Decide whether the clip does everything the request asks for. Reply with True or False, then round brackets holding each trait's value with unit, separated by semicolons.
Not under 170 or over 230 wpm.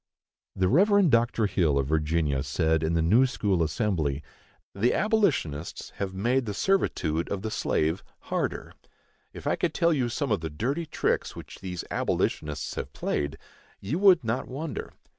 False (160 wpm)